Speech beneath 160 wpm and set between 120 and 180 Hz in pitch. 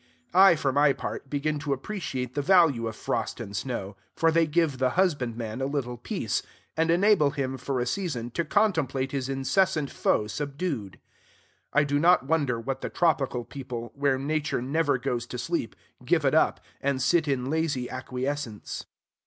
No: average, 170 wpm; medium, 140 Hz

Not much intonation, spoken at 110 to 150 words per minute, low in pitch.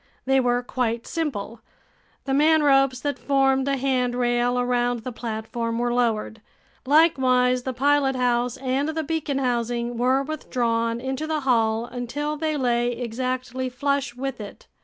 No: narrow, 2.2 semitones; average, 140 wpm; very high, 250 Hz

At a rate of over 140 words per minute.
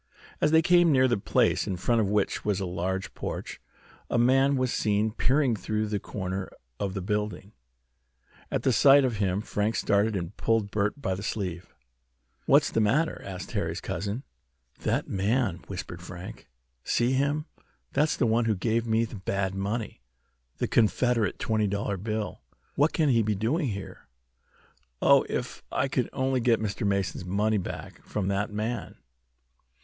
Yes: average, 165 wpm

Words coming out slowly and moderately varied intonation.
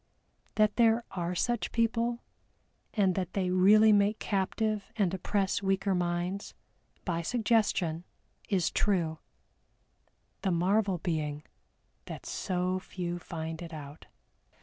Yes: slow, 115 wpm; average, 3.4 semitones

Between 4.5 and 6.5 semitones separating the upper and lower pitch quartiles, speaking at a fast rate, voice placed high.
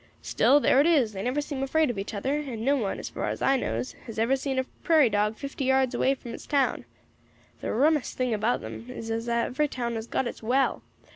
No: average, 3.4 semitones; fast, 235 wpm; very high, 255 Hz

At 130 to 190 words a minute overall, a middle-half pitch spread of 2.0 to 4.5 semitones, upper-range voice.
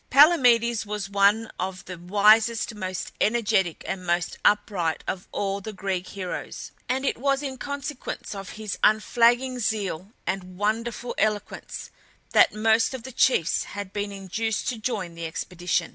Yes: average, 150 wpm; average, 3.7 semitones; high, 210 Hz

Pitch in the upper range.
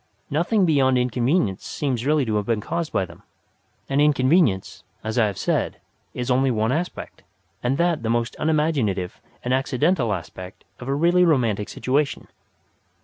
No: low, 130 Hz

